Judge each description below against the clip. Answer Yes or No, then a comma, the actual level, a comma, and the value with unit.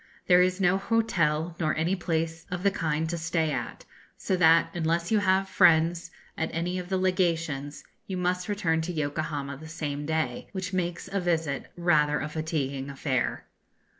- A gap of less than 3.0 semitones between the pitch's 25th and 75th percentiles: Yes, narrow, 2.6 semitones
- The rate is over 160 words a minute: Yes, average, 170 wpm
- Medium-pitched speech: Yes, medium, 165 Hz